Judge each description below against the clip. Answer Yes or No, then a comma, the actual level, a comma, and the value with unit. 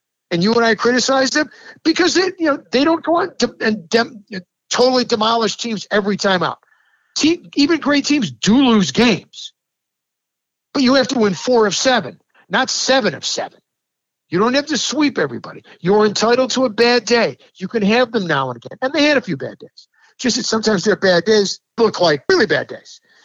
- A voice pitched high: Yes, high, 235 Hz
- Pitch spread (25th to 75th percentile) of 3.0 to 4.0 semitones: No, average, 4.8 semitones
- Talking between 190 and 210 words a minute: Yes, average, 200 wpm